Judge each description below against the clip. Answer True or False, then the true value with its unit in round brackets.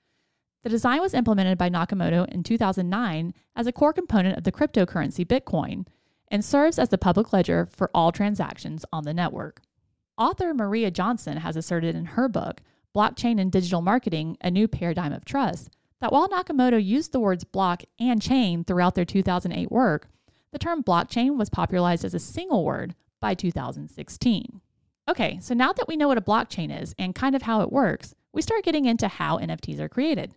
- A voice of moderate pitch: False (205 Hz)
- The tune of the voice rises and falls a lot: True (5.9 semitones)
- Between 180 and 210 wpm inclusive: True (185 wpm)